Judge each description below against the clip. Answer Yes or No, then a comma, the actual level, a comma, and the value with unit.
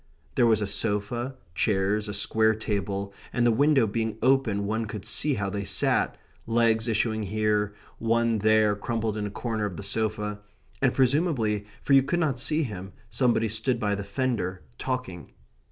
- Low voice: Yes, low, 110 Hz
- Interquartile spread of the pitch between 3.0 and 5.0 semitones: No, narrow, 2.6 semitones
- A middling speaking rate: Yes, average, 170 wpm